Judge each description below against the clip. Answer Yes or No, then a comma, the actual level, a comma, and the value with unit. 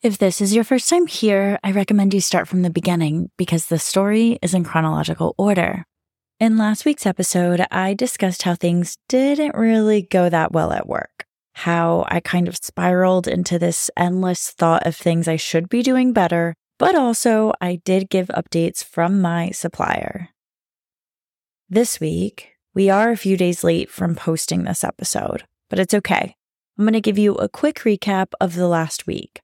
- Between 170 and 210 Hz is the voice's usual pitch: Yes, medium, 185 Hz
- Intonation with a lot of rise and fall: No, average, 3.9 semitones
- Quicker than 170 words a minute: Yes, average, 180 wpm